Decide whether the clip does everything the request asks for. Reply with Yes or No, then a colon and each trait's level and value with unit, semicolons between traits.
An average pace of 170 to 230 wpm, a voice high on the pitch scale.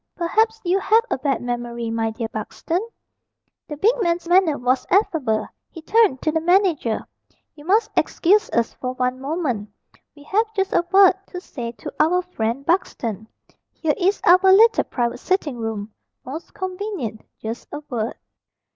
No: average, 160 wpm; very high, 315 Hz